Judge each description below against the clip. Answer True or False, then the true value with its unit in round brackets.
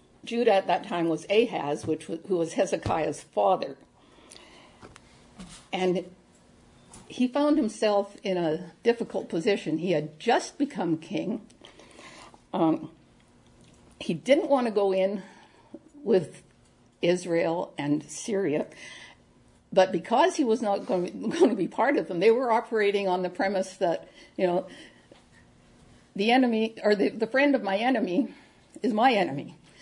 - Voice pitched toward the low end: False (195 Hz)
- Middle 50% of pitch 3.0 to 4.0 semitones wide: False (4.8 semitones)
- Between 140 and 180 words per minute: True (145 wpm)